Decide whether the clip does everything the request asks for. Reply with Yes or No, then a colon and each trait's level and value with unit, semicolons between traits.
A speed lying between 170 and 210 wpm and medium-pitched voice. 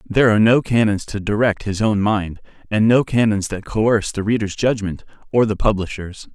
No: average, 190 wpm; low, 105 Hz